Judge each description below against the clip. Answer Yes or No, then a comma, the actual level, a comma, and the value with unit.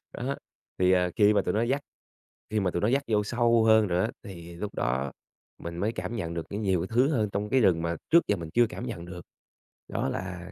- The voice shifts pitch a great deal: No, average, 4.7 semitones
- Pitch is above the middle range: No, low, 100 Hz